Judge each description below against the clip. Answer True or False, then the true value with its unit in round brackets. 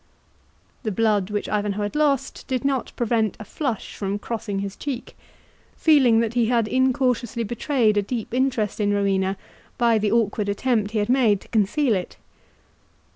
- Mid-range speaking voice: False (225 Hz)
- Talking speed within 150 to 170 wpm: True (165 wpm)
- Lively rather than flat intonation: False (3.4 semitones)